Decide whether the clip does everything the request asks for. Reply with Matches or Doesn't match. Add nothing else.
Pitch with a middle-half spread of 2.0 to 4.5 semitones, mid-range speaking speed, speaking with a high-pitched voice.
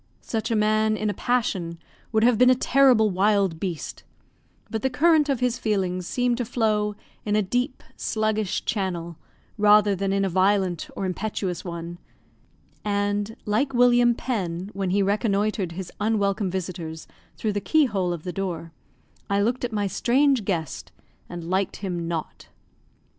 Matches